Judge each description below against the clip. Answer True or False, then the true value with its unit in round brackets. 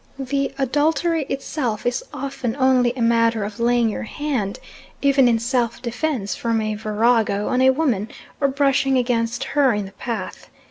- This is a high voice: True (245 Hz)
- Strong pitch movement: False (3.3 semitones)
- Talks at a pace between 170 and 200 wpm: False (160 wpm)